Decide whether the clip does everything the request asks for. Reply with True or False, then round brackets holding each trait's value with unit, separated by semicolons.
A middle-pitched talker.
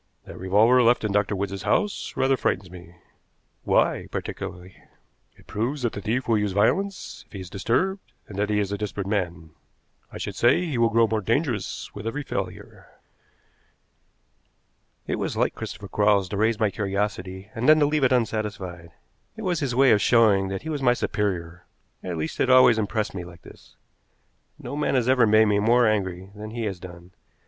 False (105 Hz)